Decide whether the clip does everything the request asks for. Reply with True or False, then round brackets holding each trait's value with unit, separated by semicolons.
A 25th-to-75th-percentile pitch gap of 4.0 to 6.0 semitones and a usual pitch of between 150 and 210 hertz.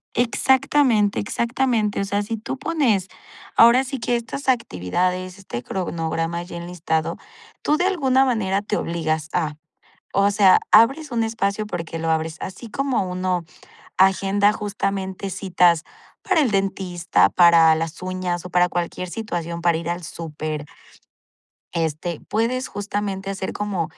True (4.7 semitones; 190 Hz)